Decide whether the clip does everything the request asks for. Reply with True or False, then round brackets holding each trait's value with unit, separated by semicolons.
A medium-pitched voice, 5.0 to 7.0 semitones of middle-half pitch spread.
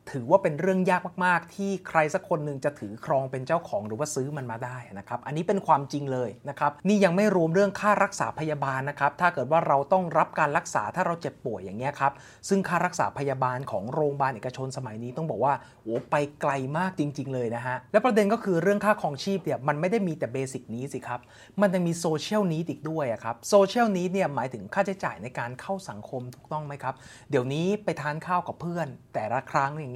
True (150 Hz; 5.5 semitones)